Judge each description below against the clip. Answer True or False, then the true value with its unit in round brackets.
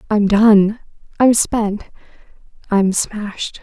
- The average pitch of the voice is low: False (210 Hz)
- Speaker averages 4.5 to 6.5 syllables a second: False (3.1 syllables/s)